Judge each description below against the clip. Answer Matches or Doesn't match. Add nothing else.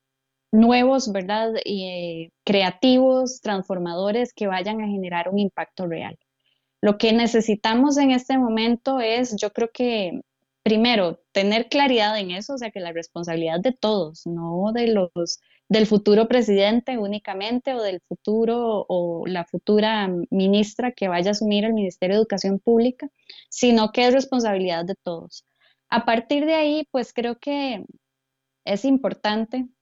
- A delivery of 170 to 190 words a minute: Doesn't match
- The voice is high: Matches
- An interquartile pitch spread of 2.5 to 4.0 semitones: Doesn't match